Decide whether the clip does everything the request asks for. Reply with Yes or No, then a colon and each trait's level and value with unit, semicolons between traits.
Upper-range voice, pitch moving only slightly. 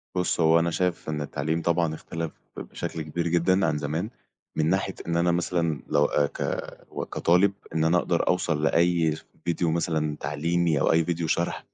No: very low, 85 Hz; narrow, 1.8 semitones